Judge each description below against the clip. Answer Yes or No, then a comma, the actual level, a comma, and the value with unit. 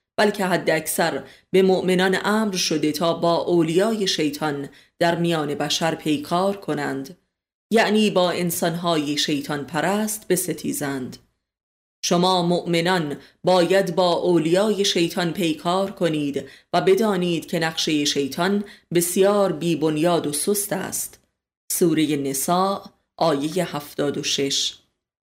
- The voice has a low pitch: No, medium, 170 Hz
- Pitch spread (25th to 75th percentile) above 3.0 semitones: Yes, average, 3.7 semitones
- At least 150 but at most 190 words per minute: No, slow, 105 wpm